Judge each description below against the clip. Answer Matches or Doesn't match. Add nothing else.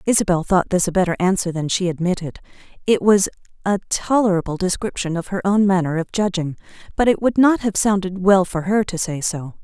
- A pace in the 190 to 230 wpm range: Matches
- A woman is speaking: Matches